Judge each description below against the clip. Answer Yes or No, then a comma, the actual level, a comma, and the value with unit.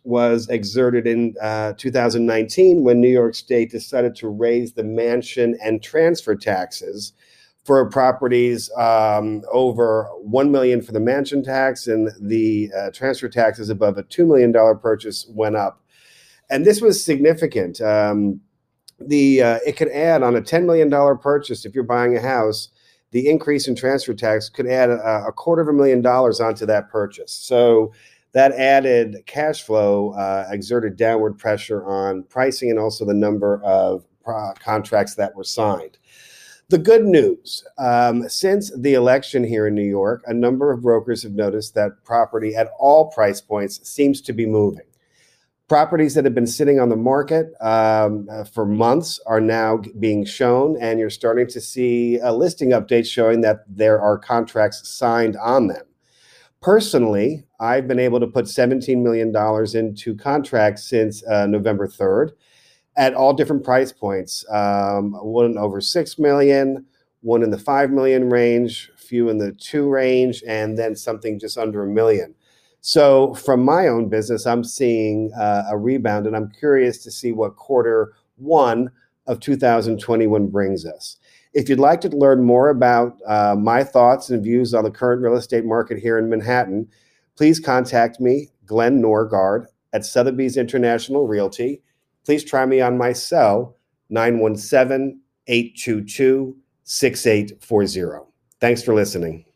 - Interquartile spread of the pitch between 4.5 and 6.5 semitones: No, average, 3.4 semitones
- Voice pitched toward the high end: No, low, 120 Hz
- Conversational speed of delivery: Yes, average, 160 wpm